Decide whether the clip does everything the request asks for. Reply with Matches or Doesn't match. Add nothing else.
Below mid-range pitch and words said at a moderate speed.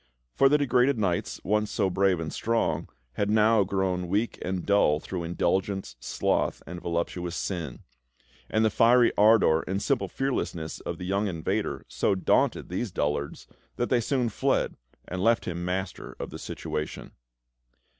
Matches